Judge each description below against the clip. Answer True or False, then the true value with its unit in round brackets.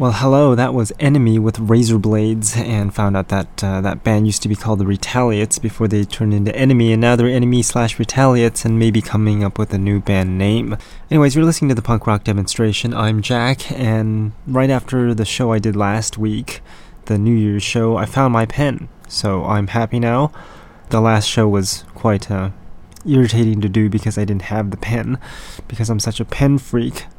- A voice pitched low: True (110 Hz)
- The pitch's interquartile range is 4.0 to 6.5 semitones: False (2.6 semitones)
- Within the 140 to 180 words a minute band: False (205 wpm)